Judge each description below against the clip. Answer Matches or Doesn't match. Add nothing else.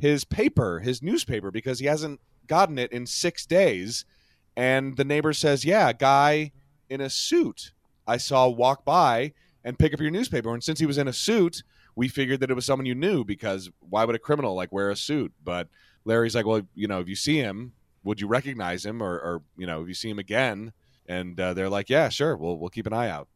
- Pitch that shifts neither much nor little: Doesn't match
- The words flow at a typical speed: Doesn't match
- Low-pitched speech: Matches